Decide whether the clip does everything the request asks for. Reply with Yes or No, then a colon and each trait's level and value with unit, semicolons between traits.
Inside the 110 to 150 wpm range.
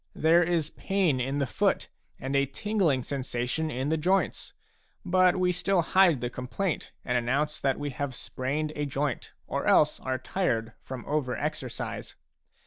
No: average, 165 wpm